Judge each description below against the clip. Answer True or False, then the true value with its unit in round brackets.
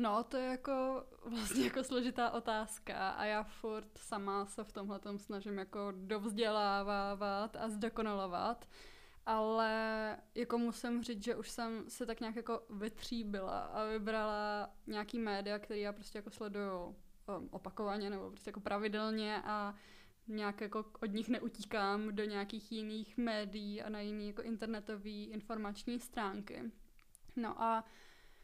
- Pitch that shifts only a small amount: True (1.7 semitones)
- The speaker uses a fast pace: False (135 wpm)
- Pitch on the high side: True (215 Hz)